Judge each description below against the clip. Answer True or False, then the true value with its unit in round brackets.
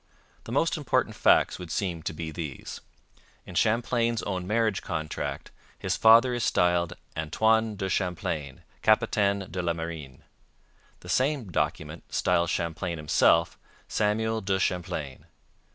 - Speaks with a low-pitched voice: True (90 Hz)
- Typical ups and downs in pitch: True (4.9 semitones)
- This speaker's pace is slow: True (130 wpm)